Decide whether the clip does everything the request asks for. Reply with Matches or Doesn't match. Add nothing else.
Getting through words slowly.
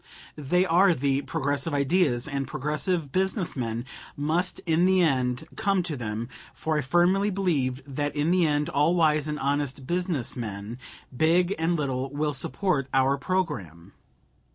Doesn't match